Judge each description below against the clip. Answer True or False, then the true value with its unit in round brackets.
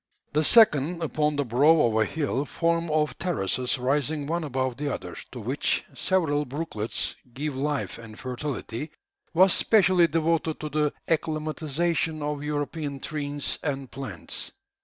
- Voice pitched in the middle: True (150 Hz)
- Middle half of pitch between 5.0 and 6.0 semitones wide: False (2.9 semitones)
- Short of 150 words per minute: True (140 wpm)